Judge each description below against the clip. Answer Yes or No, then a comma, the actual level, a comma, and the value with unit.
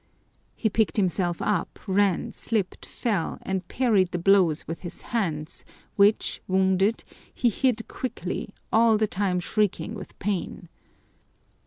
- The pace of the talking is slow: Yes, slow, 130 wpm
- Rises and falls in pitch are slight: No, average, 3.3 semitones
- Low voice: No, high, 195 Hz